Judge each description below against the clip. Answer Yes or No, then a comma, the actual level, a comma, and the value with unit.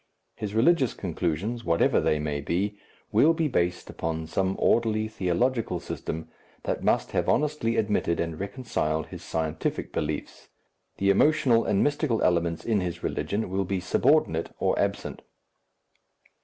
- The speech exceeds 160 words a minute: No, average, 140 wpm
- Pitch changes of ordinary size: No, wide, 5.7 semitones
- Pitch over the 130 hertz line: No, low, 100 Hz